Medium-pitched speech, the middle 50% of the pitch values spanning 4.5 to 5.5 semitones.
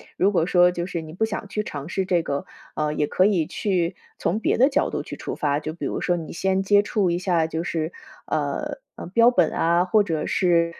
No: medium, 175 Hz; average, 3.4 semitones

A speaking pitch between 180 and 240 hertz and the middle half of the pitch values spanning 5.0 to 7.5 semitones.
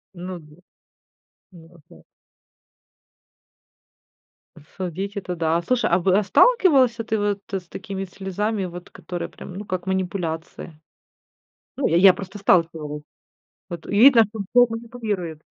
No: high, 190 Hz; average, 3.5 semitones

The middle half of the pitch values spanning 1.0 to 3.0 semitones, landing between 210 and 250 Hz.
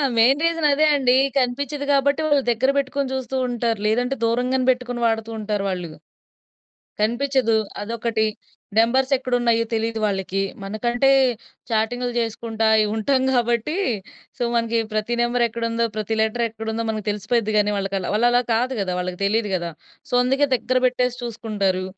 Yes: narrow, 2.6 semitones; high, 235 Hz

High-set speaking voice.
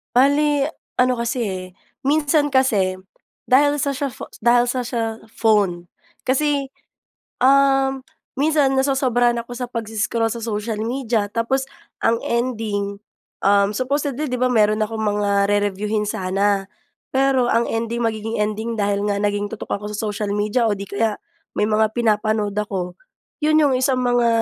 Yes: high, 230 Hz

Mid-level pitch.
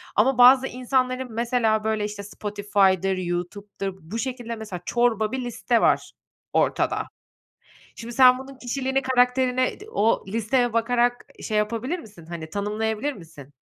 No: high, 230 Hz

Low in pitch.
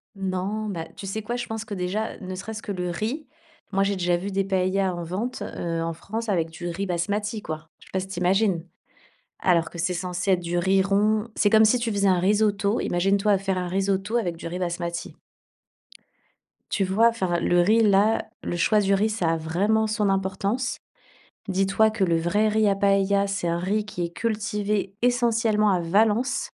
No: high, 195 Hz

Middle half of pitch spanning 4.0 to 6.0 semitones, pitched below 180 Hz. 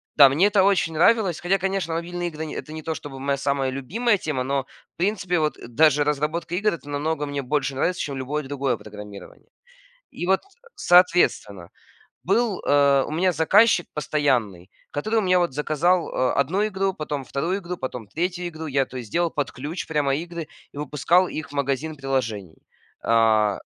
Yes: average, 4.6 semitones; medium, 150 Hz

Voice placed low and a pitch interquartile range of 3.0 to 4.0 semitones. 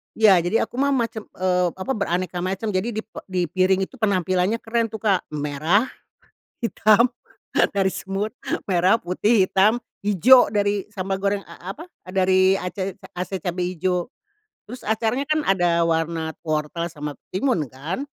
No: high, 190 Hz; average, 3.4 semitones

